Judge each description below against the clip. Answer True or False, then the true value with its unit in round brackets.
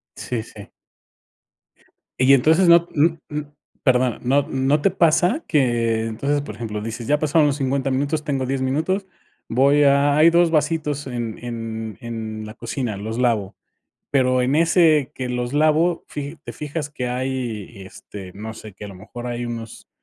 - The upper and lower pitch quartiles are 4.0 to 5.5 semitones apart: True (4.4 semitones)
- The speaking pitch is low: True (130 Hz)